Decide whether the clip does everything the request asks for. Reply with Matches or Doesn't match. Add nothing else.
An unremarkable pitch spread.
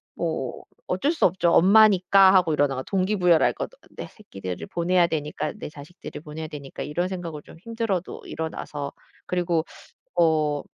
Matches